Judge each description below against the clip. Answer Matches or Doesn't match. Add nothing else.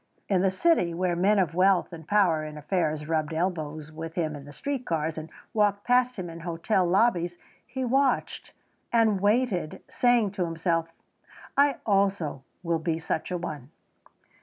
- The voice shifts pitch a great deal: Doesn't match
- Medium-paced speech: Matches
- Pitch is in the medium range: Matches